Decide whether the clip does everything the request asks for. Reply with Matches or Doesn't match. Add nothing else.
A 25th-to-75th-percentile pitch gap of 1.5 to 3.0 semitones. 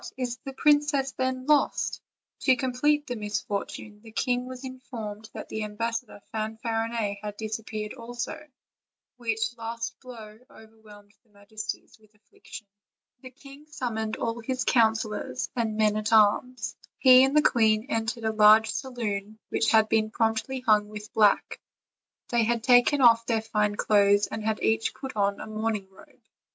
Matches